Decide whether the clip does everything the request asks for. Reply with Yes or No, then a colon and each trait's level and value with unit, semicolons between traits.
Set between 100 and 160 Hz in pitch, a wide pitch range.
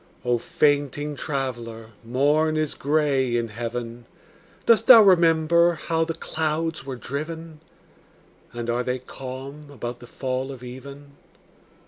No: medium, 140 Hz; average, 4.2 semitones